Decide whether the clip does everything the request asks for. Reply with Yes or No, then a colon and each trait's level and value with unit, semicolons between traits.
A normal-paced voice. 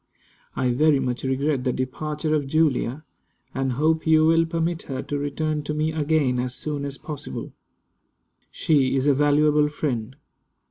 Yes: average, 155 wpm